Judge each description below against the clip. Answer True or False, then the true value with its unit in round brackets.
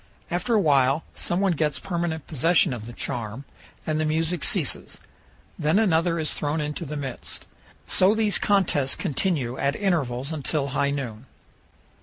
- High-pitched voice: False (155 Hz)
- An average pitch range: True (4.0 semitones)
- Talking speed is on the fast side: False (155 wpm)